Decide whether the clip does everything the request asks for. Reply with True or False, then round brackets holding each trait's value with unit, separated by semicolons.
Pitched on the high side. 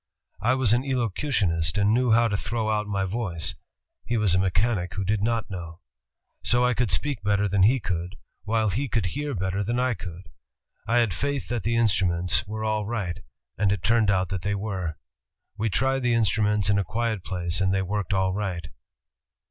False (105 Hz)